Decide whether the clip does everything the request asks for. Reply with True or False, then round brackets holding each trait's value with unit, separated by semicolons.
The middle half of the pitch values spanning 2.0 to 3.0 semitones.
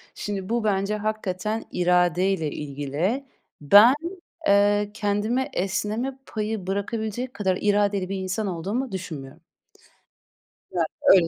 True (2.7 semitones)